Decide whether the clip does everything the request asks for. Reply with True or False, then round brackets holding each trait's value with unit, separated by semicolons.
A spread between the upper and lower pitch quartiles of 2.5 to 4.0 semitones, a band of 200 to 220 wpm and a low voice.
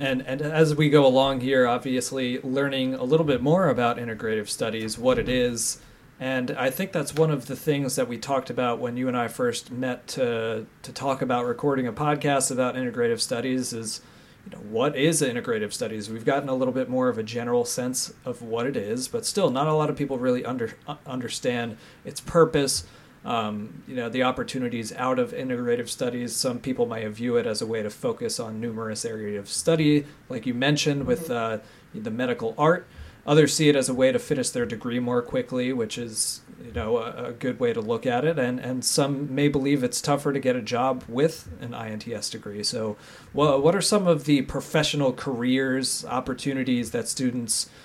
True (3.7 semitones; 205 wpm; 130 Hz)